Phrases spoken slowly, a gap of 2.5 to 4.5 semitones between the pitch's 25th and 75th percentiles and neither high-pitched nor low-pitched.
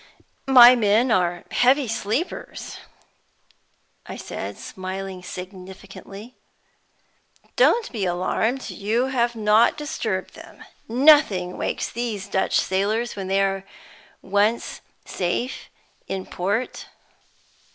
No: slow, 100 wpm; average, 4.1 semitones; high, 210 Hz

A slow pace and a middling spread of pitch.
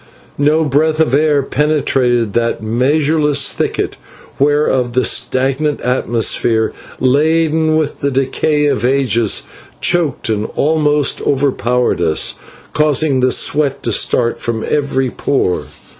Yes: slow, 115 wpm; average, 3.5 semitones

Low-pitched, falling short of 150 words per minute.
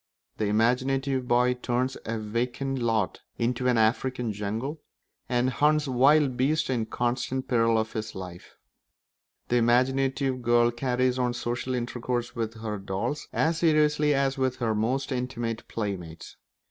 Yes: low, 125 Hz; average, 140 wpm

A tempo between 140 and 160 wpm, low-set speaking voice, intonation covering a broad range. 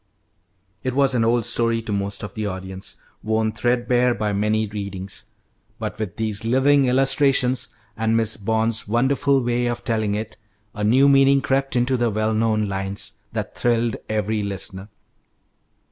No: average, 155 wpm; low, 115 Hz; average, 3.1 semitones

